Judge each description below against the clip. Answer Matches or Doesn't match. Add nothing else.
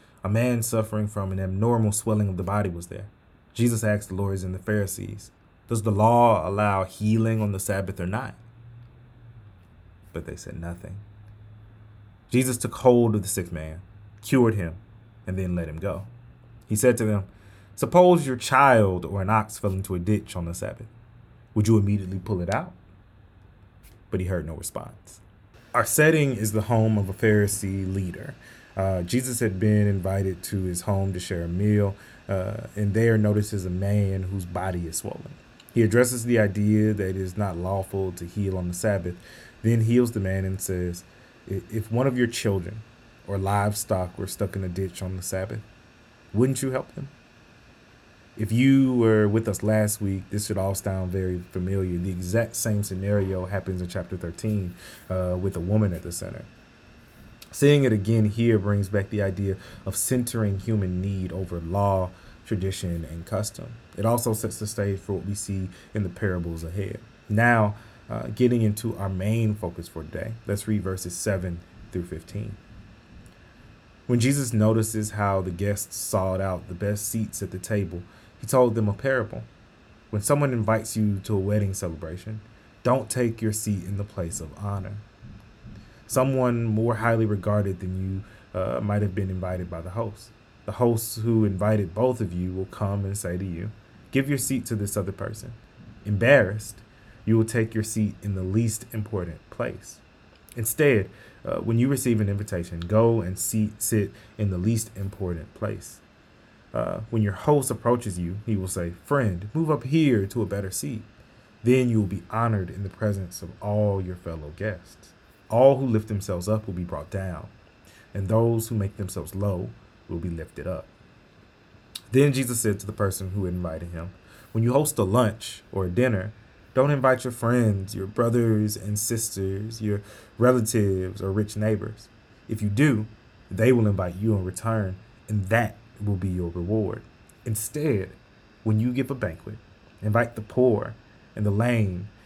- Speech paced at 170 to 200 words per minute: Matches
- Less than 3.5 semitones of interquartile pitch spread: Matches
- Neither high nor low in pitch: Doesn't match